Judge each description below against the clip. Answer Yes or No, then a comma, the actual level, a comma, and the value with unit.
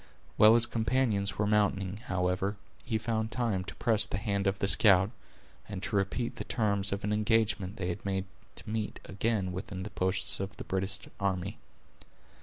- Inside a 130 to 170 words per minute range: No, average, 180 wpm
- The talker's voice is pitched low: Yes, low, 100 Hz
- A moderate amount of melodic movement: No, narrow, 2.3 semitones